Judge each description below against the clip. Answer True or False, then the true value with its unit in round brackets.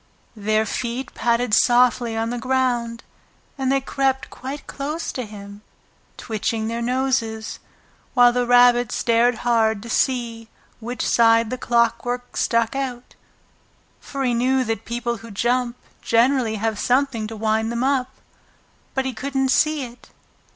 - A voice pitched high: True (240 Hz)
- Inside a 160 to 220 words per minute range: False (145 wpm)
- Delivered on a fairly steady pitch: True (2.2 semitones)